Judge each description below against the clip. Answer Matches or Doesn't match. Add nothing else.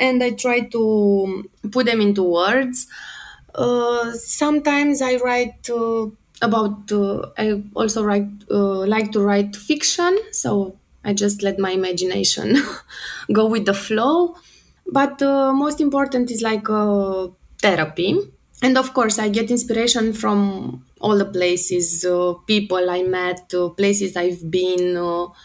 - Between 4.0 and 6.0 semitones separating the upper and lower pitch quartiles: Matches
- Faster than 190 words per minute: Doesn't match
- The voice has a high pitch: Matches